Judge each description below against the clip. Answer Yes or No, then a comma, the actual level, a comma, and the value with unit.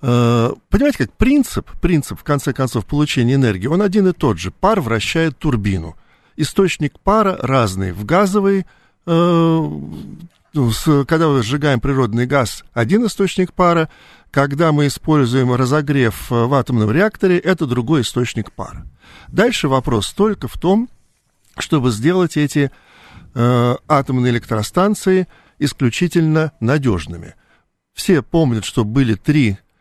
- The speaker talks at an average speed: Yes, average, 120 wpm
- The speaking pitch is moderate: Yes, medium, 145 Hz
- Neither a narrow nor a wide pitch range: No, wide, 6.0 semitones